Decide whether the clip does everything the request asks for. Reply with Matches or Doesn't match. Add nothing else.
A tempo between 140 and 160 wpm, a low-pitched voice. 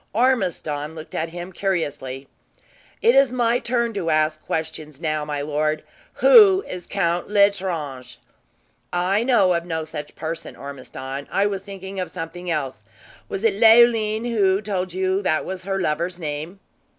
Doesn't match